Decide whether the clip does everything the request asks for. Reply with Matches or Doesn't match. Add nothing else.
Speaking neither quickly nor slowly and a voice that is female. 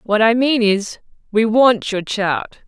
Matches